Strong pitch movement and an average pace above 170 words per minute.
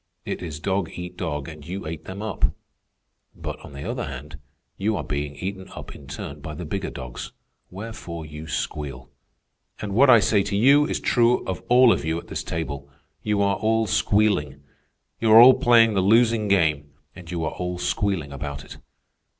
Yes: wide, 6.1 semitones; average, 190 wpm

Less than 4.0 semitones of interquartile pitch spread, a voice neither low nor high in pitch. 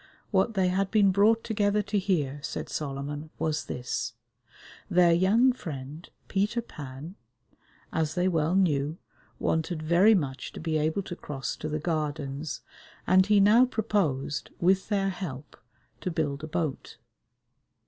No: average, 4.9 semitones; medium, 170 Hz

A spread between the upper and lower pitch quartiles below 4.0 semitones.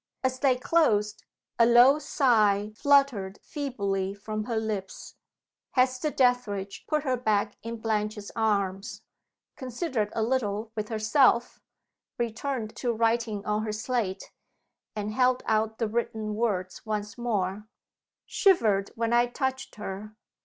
Yes: average, 3.1 semitones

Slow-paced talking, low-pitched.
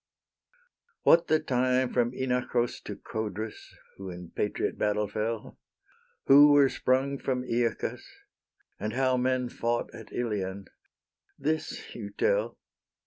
Yes: slow, 120 wpm; low, 125 Hz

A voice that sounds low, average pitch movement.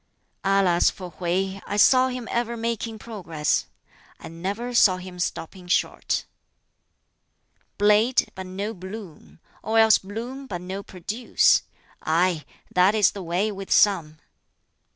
No: high, 195 Hz; average, 3.6 semitones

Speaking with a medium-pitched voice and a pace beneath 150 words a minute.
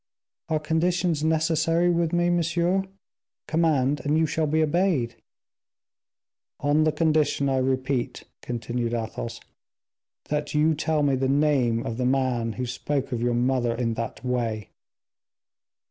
Yes: medium, 145 Hz; slow, 135 wpm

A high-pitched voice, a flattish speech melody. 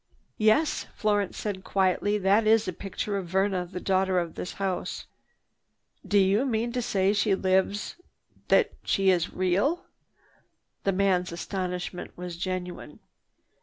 Yes: high, 195 Hz; narrow, 2.1 semitones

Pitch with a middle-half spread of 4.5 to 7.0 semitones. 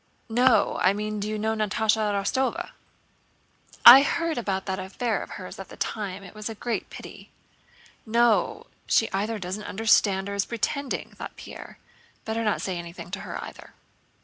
No: average, 2.7 semitones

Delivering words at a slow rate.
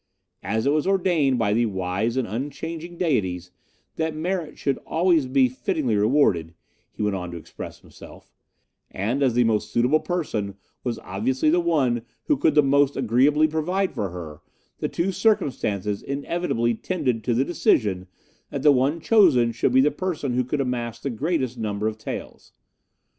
No: average, 170 wpm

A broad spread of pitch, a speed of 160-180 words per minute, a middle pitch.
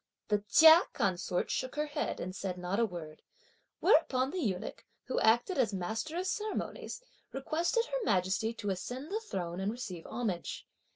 No: wide, 8.8 semitones; average, 165 wpm; high, 230 Hz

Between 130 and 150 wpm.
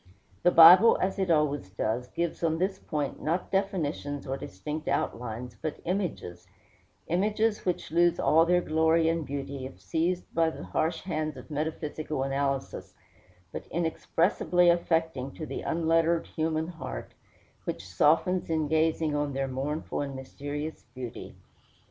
Yes: average, 140 wpm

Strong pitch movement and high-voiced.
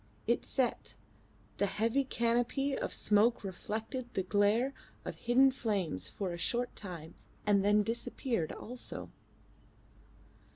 No: average, 3.5 semitones; high, 225 Hz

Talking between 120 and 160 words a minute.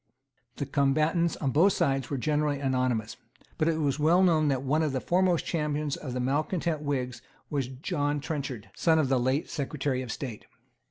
No: average, 180 wpm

